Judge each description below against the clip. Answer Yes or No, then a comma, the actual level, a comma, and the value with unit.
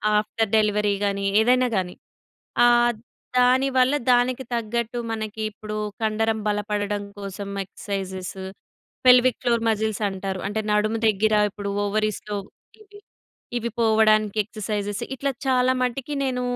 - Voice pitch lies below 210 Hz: No, high, 215 Hz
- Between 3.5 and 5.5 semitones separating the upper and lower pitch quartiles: No, average, 2.8 semitones